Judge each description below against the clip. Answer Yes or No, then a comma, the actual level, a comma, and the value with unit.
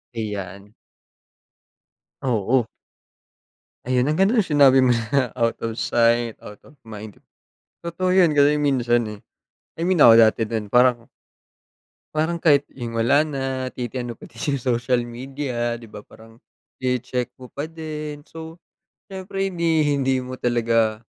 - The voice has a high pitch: No, low, 125 Hz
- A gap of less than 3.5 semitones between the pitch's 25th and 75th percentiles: No, average, 4.3 semitones